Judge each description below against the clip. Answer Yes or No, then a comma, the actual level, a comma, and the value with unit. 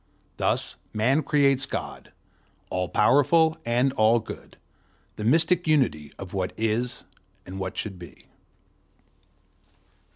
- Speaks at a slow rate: Yes, slow, 110 wpm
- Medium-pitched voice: No, low, 120 Hz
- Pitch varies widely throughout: Yes, wide, 6.5 semitones